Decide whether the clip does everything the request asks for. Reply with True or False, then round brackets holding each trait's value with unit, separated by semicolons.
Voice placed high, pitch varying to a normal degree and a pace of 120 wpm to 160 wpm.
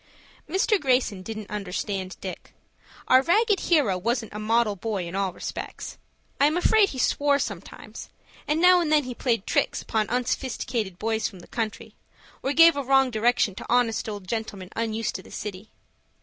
False (230 Hz; 5.0 semitones; 175 wpm)